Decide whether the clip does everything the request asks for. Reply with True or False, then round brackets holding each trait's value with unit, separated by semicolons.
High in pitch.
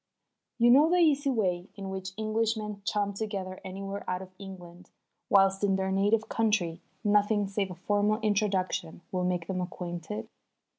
True (195 Hz)